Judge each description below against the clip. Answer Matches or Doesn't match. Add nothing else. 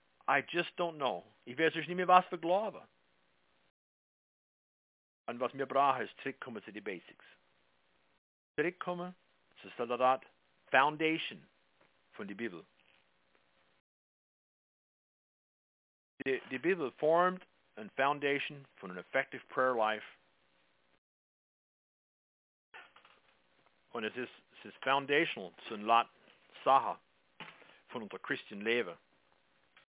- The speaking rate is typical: Doesn't match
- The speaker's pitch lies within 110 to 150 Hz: Doesn't match